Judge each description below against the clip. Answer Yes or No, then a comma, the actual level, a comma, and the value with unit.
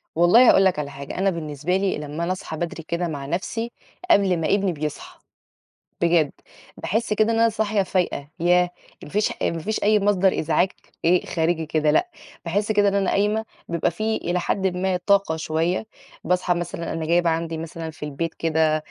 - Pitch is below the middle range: No, medium, 175 Hz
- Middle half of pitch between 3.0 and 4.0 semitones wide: Yes, average, 3.6 semitones